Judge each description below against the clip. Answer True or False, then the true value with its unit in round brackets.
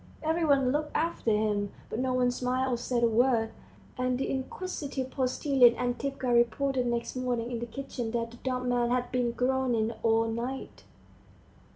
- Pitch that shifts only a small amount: True (1.9 semitones)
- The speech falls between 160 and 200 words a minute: True (170 wpm)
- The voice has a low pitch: False (250 Hz)